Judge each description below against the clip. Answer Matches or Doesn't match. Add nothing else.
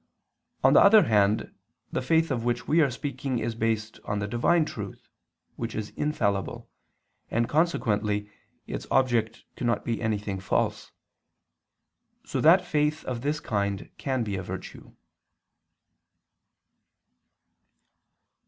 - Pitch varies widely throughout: Matches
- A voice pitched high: Doesn't match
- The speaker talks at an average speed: Doesn't match